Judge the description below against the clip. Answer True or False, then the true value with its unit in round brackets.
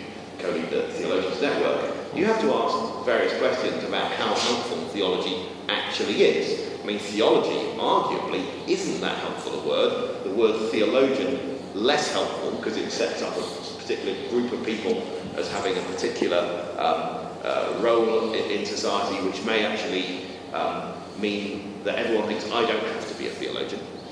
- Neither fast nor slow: True (160 wpm)